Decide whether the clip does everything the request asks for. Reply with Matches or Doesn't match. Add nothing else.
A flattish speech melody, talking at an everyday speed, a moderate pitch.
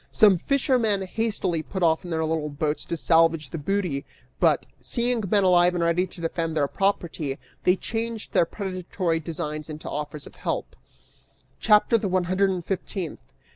Doesn't match